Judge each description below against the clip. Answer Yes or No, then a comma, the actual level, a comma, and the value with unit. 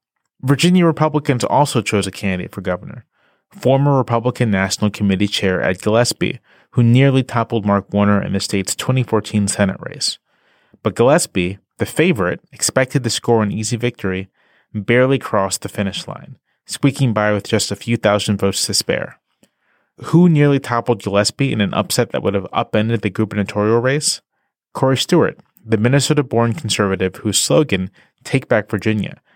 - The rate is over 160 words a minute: No, average, 155 wpm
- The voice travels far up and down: No, average, 4.5 semitones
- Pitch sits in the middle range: No, low, 110 Hz